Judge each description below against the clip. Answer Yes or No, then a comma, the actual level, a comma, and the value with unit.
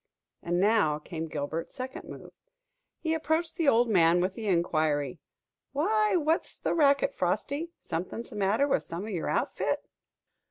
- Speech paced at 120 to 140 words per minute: No, average, 155 wpm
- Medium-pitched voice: No, high, 220 Hz